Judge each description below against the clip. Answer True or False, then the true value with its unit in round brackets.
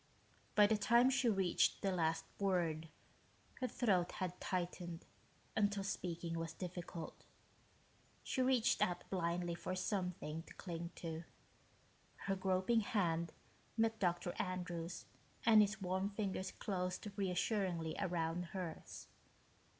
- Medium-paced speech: False (120 wpm)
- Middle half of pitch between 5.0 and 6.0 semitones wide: False (2.9 semitones)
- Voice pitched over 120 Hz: True (185 Hz)